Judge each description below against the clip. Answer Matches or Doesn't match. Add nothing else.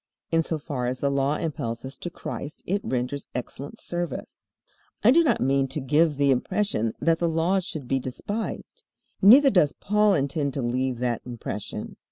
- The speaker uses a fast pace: Doesn't match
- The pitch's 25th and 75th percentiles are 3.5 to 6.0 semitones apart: Matches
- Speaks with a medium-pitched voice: Matches